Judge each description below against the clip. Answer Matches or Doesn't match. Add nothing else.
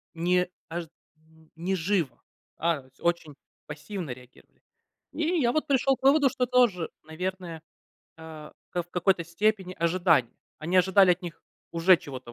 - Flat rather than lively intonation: Doesn't match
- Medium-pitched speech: Matches